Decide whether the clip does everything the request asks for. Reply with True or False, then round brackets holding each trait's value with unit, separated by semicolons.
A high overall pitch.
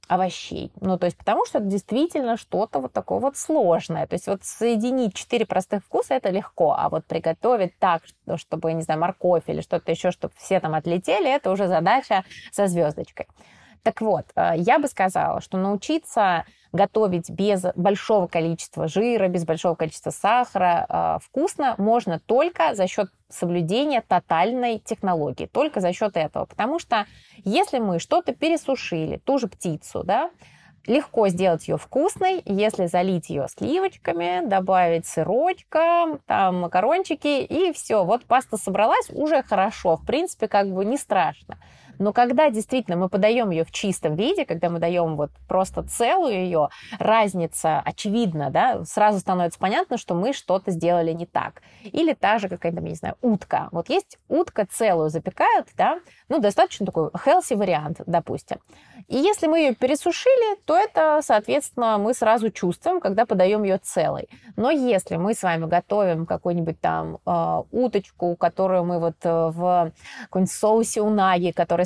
True (200 Hz)